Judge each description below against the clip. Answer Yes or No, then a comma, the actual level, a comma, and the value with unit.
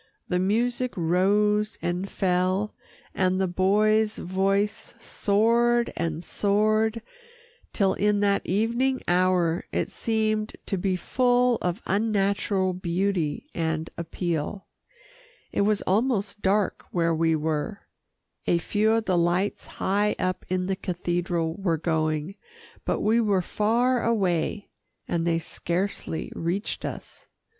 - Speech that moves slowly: Yes, slow, 120 wpm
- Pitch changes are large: No, average, 3.5 semitones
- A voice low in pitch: No, high, 195 Hz